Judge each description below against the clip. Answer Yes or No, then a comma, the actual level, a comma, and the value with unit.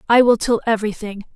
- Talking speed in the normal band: Yes, average, 180 wpm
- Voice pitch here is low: No, high, 220 Hz